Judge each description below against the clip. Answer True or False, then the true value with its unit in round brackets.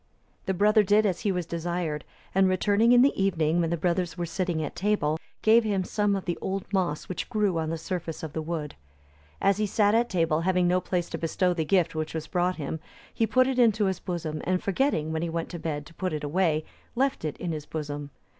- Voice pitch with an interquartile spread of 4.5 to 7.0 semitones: False (3.7 semitones)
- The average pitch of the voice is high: False (180 Hz)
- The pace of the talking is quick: True (235 wpm)